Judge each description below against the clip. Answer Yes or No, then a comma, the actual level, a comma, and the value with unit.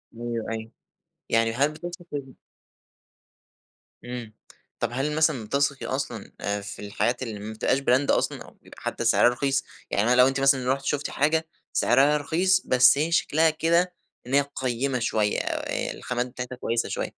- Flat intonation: No, average, 3.7 semitones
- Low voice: Yes, low, 130 Hz